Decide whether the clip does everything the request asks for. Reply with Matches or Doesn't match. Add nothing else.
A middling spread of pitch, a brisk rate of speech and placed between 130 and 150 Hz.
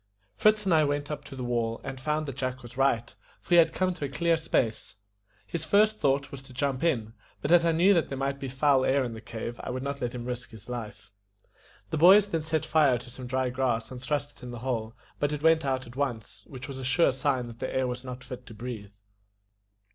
Matches